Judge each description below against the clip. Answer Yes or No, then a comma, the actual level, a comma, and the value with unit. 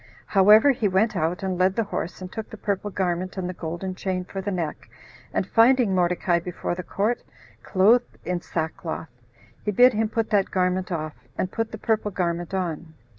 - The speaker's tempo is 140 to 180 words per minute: No, average, 190 wpm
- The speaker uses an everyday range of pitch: Yes, average, 3.0 semitones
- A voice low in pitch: No, medium, 185 Hz